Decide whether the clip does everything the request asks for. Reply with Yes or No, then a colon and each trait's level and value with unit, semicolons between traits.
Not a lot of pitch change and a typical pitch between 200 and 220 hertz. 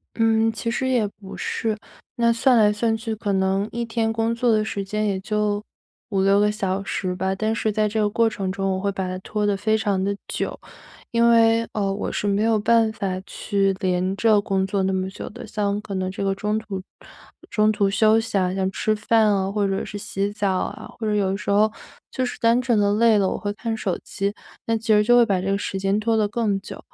Yes: narrow, 2.3 semitones; high, 210 Hz